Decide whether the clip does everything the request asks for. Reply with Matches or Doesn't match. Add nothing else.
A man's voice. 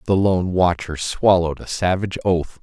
Matches